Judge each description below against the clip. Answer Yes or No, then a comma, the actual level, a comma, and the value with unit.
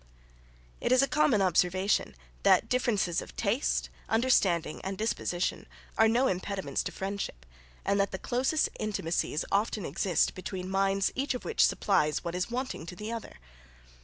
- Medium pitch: No, high, 195 Hz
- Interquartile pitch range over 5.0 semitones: No, average, 4.4 semitones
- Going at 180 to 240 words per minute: No, average, 155 wpm